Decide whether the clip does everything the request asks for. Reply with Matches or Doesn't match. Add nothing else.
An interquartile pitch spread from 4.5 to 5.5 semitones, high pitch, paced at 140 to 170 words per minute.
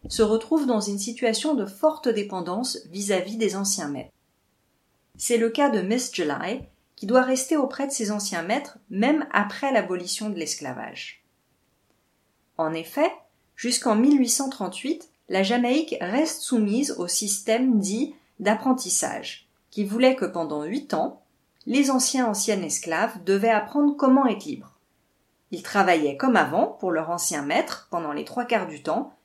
Matches